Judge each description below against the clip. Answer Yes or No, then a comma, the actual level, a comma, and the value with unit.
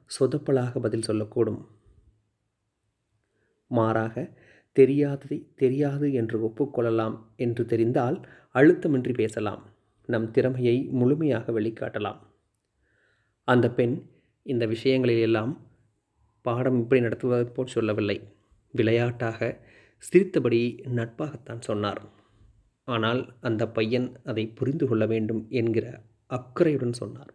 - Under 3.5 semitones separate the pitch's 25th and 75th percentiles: Yes, narrow, 2.6 semitones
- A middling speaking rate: Yes, average, 85 wpm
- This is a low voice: Yes, low, 115 Hz